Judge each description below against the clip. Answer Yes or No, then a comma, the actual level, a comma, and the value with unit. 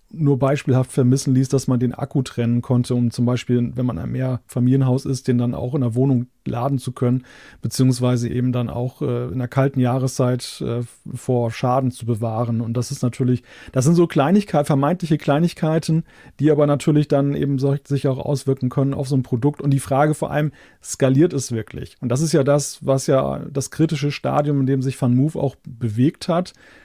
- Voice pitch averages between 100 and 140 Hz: Yes, low, 135 Hz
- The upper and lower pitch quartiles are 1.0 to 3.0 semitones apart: Yes, narrow, 2.5 semitones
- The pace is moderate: No, fast, 200 wpm